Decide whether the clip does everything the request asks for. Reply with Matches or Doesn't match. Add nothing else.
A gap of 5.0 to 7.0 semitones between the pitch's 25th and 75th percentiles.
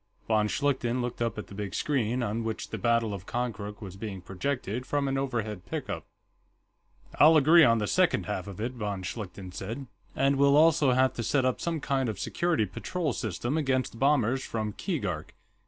Doesn't match